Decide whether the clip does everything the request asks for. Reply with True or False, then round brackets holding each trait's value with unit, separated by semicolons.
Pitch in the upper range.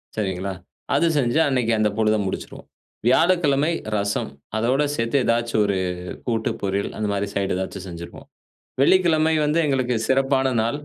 False (115 Hz)